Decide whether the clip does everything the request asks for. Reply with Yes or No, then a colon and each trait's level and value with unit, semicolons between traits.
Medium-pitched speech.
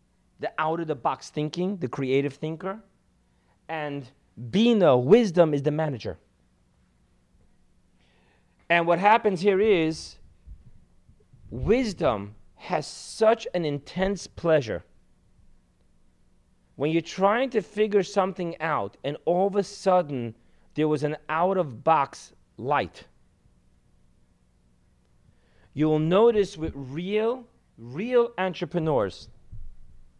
Yes: medium, 155 Hz